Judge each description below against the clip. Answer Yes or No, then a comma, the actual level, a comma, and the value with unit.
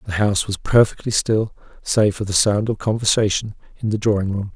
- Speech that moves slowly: No, average, 200 wpm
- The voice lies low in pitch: Yes, low, 105 Hz